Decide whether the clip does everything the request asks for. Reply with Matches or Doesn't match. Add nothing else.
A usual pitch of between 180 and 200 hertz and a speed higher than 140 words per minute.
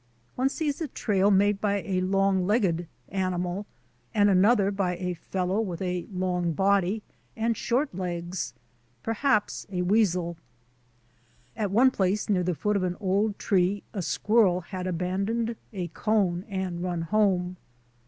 Matches